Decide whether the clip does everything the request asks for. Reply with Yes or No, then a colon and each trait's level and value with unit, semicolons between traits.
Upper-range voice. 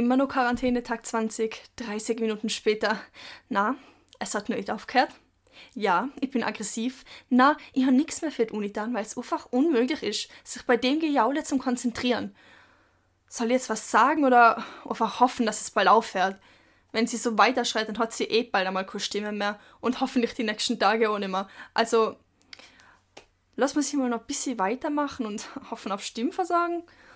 Yes: high, 240 Hz